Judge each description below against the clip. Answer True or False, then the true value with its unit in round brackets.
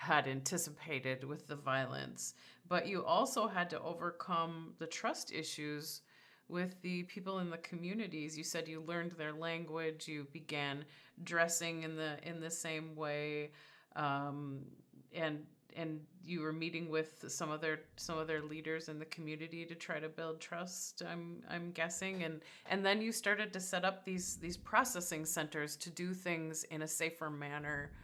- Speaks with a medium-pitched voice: True (160 Hz)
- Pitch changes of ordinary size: False (2.2 semitones)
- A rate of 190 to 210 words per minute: False (165 wpm)